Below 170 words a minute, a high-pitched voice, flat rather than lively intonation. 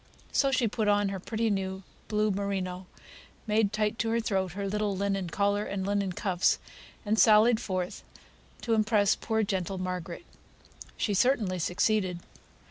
Yes: average, 150 wpm; high, 200 Hz; narrow, 2.3 semitones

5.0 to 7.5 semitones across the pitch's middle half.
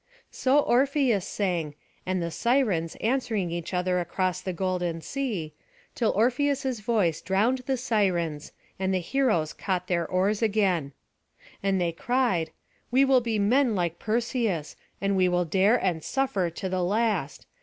Yes: wide, 5.4 semitones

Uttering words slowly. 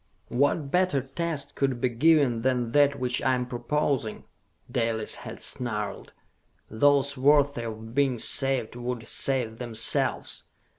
Yes: slow, 130 wpm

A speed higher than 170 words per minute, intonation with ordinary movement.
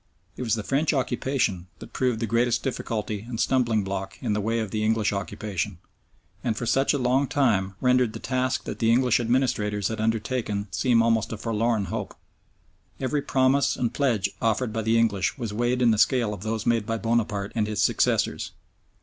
Yes: average, 190 wpm; average, 3.1 semitones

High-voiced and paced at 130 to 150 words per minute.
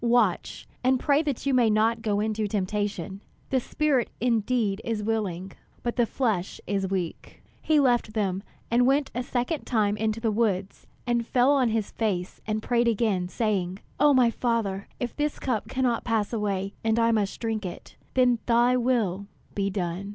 No: high, 225 Hz; average, 175 wpm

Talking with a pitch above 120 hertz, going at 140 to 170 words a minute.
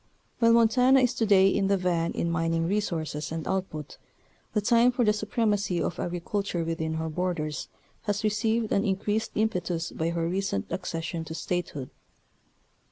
Yes: medium, 185 Hz; average, 165 wpm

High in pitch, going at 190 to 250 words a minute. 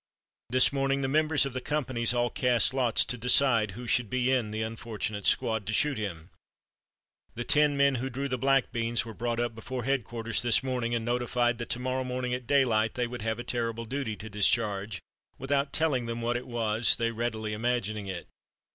No: low, 120 Hz; average, 200 wpm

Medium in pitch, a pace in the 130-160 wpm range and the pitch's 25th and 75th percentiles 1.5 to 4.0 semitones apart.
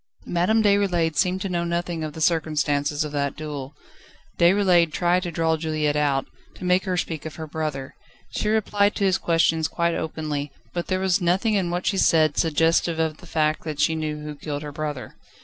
No: medium, 160 Hz; average, 200 wpm; average, 2.9 semitones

